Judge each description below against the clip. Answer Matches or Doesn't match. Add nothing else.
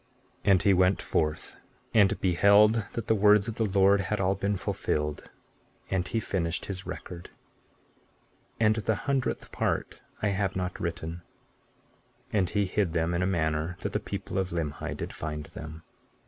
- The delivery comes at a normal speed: Matches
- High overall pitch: Doesn't match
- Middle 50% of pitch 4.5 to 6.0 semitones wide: Doesn't match